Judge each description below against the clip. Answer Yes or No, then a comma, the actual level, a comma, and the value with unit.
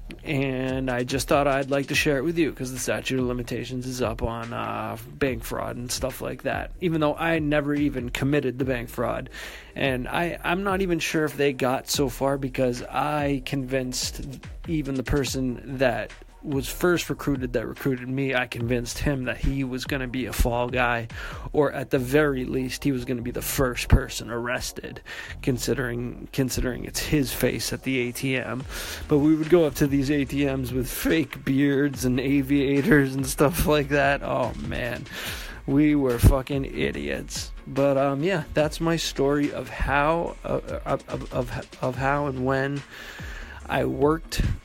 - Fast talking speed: No, average, 175 wpm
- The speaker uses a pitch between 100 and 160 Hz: Yes, low, 135 Hz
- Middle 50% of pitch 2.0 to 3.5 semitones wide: Yes, narrow, 2.5 semitones